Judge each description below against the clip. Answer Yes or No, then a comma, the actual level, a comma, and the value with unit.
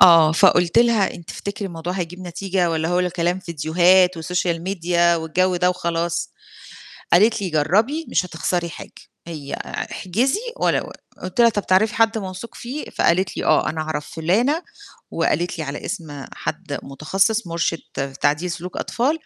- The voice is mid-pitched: Yes, medium, 180 Hz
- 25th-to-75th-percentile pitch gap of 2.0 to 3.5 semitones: Yes, average, 2.9 semitones